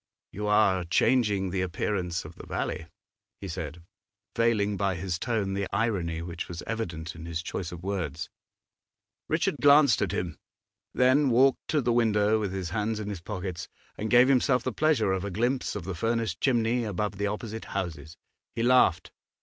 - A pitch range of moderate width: Yes, average, 4.6 semitones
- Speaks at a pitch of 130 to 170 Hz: No, low, 105 Hz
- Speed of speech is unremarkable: Yes, average, 175 wpm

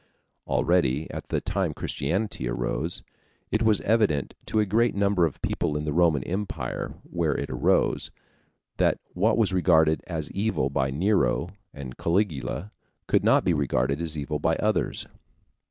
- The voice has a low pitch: Yes, very low, 85 Hz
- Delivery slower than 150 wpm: No, average, 155 wpm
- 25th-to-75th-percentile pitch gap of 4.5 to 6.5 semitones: Yes, wide, 5.6 semitones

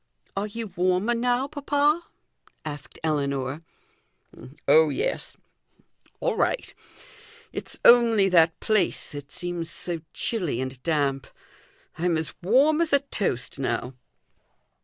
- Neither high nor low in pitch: Yes, medium, 180 Hz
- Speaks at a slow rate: Yes, slow, 115 wpm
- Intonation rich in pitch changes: Yes, wide, 8.6 semitones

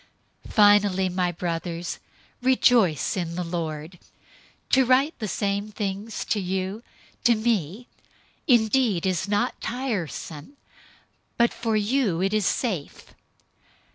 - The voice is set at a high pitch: Yes, high, 200 Hz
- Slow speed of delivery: Yes, slow, 115 wpm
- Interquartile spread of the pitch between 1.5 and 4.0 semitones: No, average, 4.6 semitones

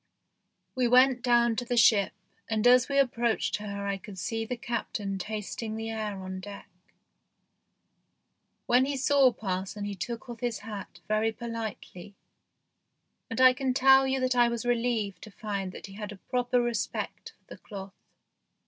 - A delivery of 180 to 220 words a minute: No, average, 165 wpm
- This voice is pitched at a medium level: No, high, 225 Hz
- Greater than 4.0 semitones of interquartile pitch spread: No, average, 3.2 semitones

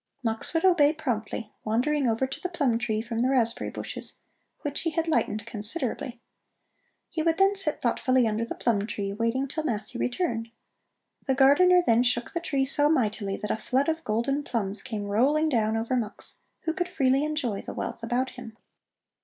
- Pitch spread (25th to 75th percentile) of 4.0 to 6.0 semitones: Yes, average, 5.1 semitones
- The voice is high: Yes, very high, 250 Hz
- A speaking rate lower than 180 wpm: No, average, 185 wpm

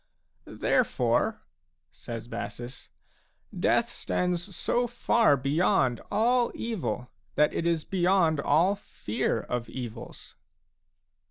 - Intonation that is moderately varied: No, wide, 7.9 semitones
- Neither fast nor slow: No, slow, 105 wpm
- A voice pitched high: No, medium, 165 Hz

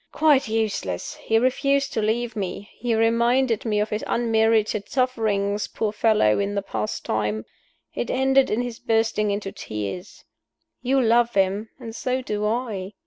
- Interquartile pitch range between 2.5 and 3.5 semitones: Yes, average, 3.1 semitones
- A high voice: Yes, high, 220 Hz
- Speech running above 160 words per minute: No, average, 155 wpm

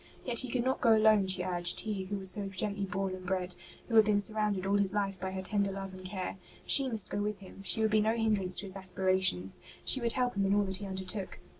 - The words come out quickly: Yes, fast, 265 wpm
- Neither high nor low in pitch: No, high, 195 Hz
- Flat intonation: Yes, narrow, 2.2 semitones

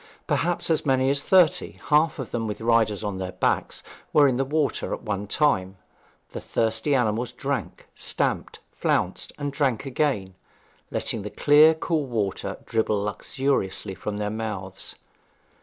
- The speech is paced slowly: No, average, 150 wpm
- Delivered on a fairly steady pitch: No, wide, 5.6 semitones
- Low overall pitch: Yes, low, 120 Hz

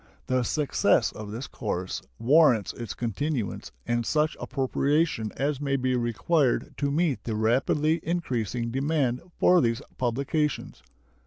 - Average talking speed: No, slow, 130 wpm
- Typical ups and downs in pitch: Yes, average, 4.3 semitones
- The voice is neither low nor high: No, low, 130 Hz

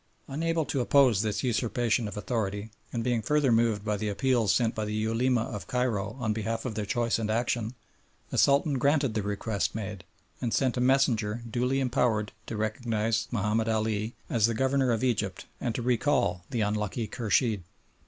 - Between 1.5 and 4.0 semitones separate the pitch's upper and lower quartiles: Yes, average, 2.8 semitones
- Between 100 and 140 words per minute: No, average, 180 wpm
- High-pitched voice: No, low, 115 Hz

